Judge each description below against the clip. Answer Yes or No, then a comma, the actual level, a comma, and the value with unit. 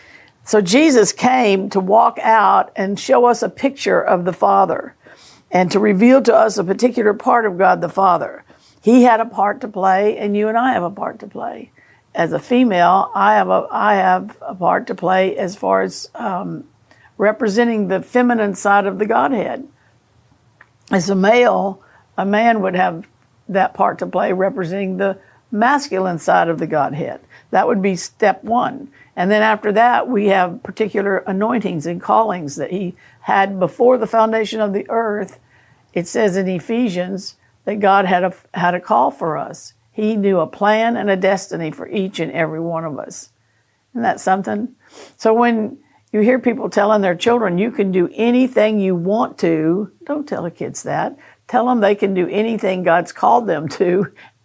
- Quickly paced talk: No, average, 185 wpm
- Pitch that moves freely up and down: No, average, 3.2 semitones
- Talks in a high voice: Yes, high, 200 Hz